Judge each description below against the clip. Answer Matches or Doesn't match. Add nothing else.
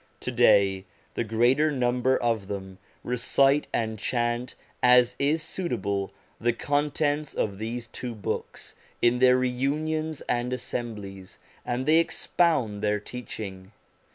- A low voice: Matches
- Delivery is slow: Matches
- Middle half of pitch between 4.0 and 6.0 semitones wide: Matches